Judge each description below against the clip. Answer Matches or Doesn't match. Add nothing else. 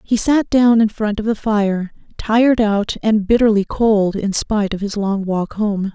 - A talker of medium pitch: Doesn't match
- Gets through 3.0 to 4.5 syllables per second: Matches